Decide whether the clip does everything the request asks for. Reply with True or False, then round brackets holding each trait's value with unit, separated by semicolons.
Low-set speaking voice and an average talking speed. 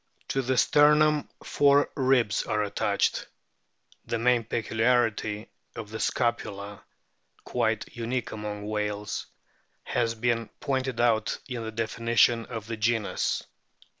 False (115 Hz; 115 wpm)